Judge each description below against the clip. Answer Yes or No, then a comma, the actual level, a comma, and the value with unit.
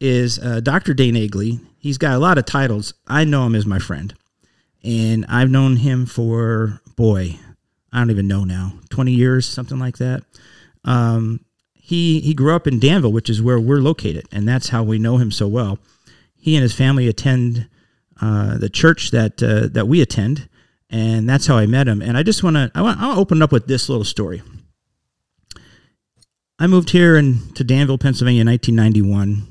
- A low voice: Yes, low, 120 Hz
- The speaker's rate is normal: Yes, average, 195 wpm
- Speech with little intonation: No, average, 3.8 semitones